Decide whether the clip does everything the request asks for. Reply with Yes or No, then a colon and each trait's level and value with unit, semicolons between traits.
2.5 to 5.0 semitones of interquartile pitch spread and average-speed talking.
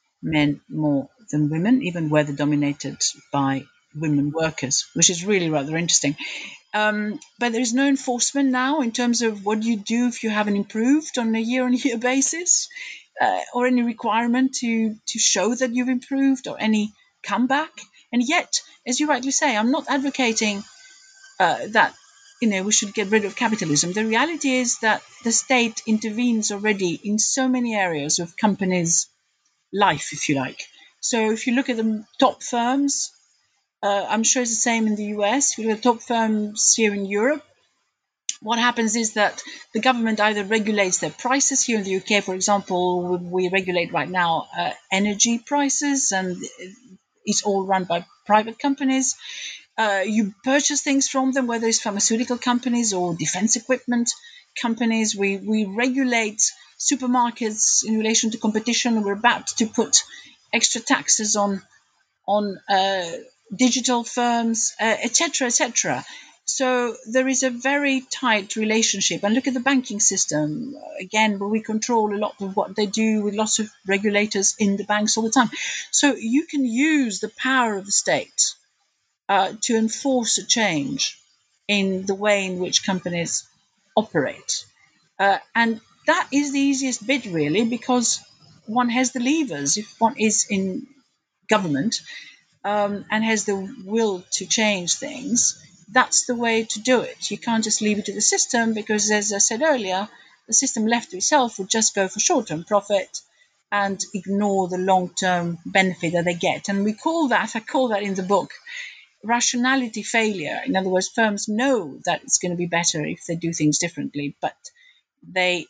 Yes: average, 4.1 semitones; average, 170 wpm